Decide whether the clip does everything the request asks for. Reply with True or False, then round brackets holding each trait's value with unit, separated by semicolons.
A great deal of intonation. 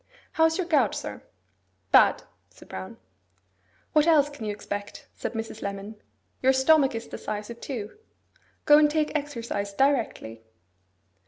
True (6.1 semitones)